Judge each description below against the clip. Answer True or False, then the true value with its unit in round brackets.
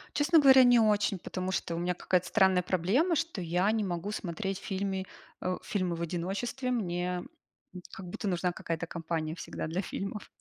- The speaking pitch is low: False (185 Hz)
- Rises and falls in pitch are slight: False (3.3 semitones)